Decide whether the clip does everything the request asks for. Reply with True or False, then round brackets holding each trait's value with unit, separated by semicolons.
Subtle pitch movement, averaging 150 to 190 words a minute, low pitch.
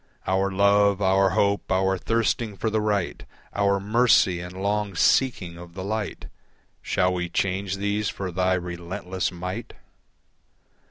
False (1.8 semitones; 140 wpm; 95 Hz)